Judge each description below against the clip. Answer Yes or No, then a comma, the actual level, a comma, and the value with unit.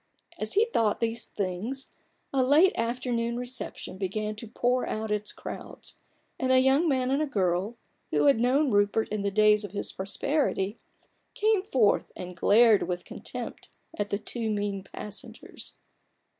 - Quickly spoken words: No, average, 155 wpm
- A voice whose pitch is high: Yes, high, 225 Hz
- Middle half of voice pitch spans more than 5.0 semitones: No, average, 4.1 semitones